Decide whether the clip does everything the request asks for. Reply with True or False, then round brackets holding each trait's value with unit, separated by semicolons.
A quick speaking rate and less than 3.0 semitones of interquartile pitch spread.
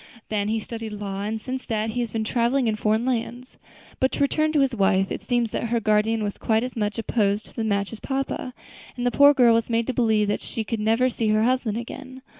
True (245 wpm; 2.6 semitones)